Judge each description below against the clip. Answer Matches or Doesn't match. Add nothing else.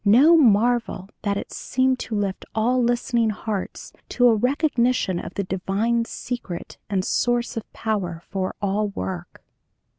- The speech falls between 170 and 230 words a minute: Doesn't match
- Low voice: Doesn't match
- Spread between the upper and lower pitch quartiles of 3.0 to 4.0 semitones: Matches